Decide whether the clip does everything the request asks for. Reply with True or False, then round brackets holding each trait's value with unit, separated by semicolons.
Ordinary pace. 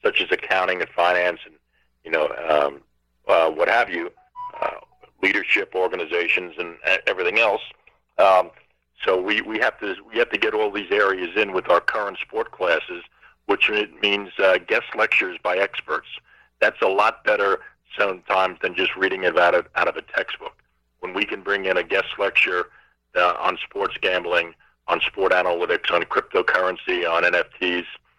True (170 wpm)